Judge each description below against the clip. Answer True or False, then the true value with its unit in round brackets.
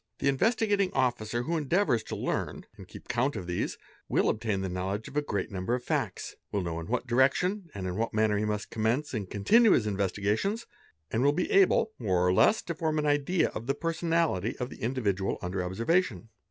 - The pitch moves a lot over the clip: True (7.8 semitones)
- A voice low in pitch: True (120 Hz)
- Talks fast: True (210 wpm)